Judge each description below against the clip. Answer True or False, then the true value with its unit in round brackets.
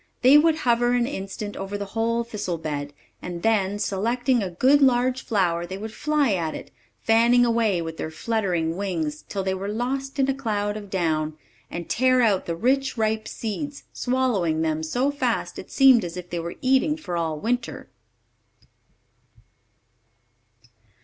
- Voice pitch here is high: True (215 Hz)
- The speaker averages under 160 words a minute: False (165 wpm)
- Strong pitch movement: True (5.9 semitones)